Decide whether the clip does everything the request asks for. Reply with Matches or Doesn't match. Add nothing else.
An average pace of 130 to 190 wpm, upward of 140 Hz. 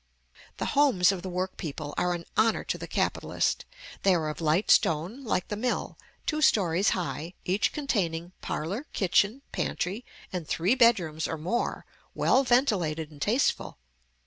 Matches